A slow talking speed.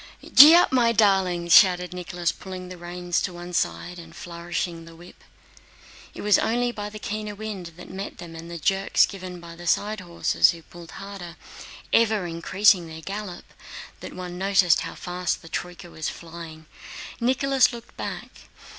No: average, 165 wpm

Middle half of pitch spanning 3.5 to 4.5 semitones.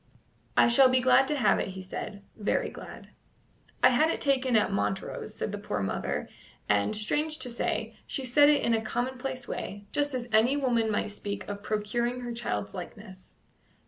Yes: average, 4.0 semitones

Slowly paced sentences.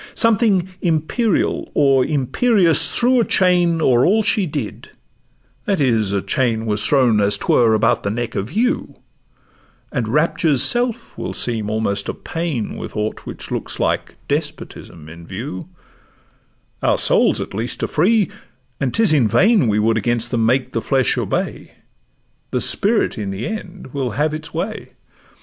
No: average, 160 wpm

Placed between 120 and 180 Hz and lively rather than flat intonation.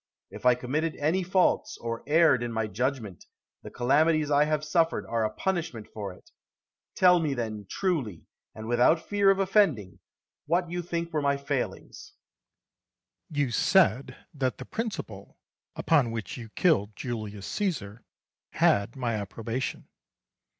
Yes: low, 135 Hz; wide, 6.7 semitones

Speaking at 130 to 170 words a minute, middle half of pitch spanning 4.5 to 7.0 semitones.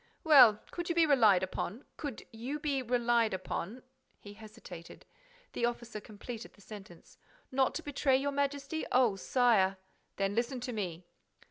Yes: average, 145 wpm; average, 4.9 semitones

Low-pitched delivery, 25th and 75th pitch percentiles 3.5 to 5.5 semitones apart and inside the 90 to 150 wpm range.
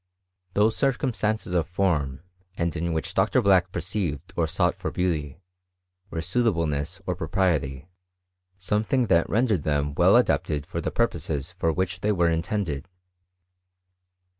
Yes: very low, 85 Hz; average, 3.9 semitones; slow, 135 wpm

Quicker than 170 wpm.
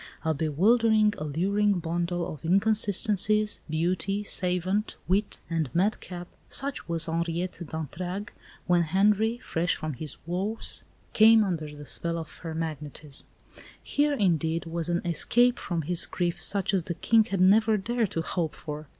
No: average, 145 wpm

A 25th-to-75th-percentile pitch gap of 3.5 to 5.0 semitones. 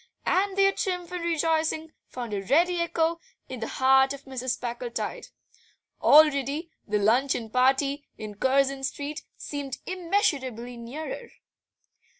Yes: average, 4.6 semitones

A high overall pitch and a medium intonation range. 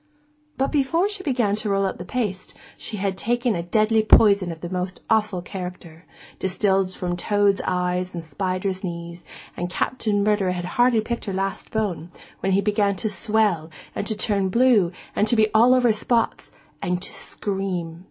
Yes: high, 200 Hz; average, 3.3 semitones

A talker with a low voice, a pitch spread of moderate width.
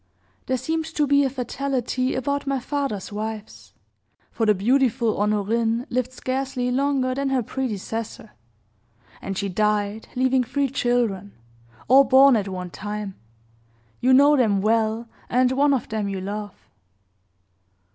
No: high, 245 Hz; average, 4.0 semitones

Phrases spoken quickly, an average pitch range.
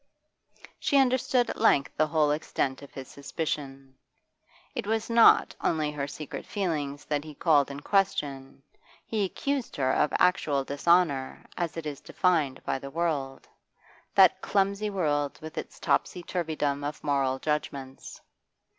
No: average, 145 wpm; average, 4.5 semitones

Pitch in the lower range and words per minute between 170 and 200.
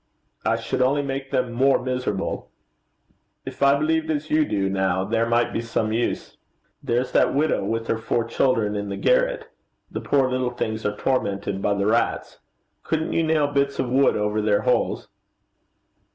Yes: low, 125 Hz; average, 175 wpm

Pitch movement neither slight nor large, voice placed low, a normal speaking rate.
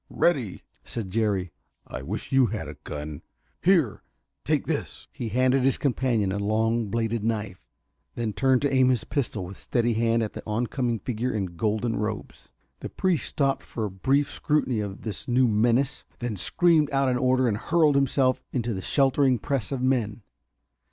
Yes: average, 3.8 semitones; low, 120 Hz; average, 175 wpm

